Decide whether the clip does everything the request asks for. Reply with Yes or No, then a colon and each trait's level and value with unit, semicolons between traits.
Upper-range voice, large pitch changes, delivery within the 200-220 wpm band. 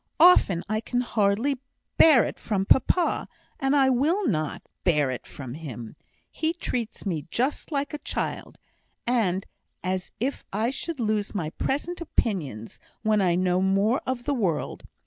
No: high, 215 Hz; wide, 6.8 semitones; average, 160 wpm